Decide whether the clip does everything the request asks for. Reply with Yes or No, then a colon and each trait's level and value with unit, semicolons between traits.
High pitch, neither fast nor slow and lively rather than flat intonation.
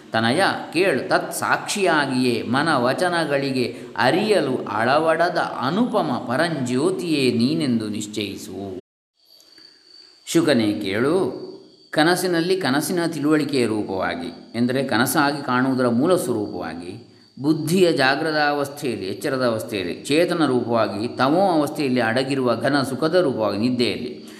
No: medium, 145 Hz; average, 90 wpm; wide, 5.7 semitones